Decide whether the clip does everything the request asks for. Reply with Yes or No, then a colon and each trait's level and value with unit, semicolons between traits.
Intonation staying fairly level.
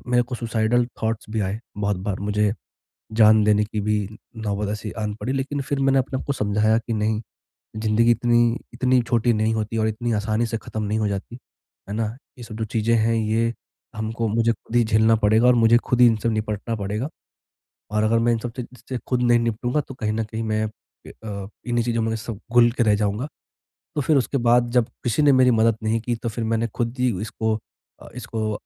Yes: narrow, 1.9 semitones